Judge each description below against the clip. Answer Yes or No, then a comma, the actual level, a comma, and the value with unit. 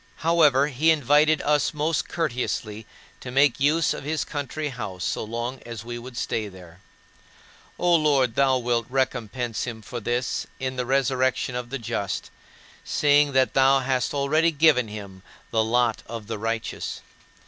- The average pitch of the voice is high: No, low, 130 Hz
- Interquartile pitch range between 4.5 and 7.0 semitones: No, average, 3.8 semitones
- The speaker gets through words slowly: No, average, 160 wpm